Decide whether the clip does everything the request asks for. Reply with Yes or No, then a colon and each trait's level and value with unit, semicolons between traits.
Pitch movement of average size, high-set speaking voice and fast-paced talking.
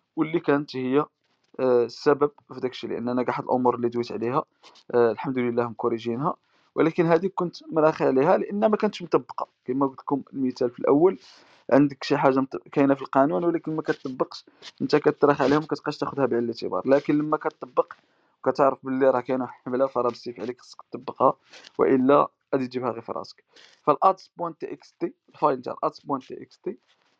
No: average, 3.3 semitones; medium, 140 Hz; fast, 155 wpm